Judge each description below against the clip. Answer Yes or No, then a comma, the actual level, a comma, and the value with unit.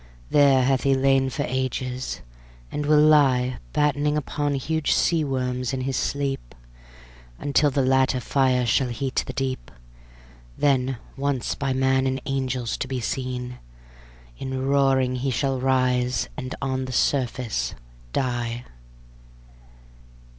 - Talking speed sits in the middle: No, slow, 130 wpm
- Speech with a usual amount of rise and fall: No, narrow, 1.4 semitones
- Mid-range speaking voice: No, low, 130 Hz